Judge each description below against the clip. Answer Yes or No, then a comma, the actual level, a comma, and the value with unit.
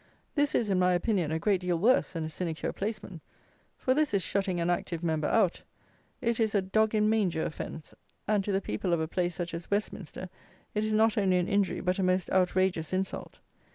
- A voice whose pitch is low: No, medium, 185 Hz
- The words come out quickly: Yes, fast, 215 wpm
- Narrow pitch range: No, average, 3.4 semitones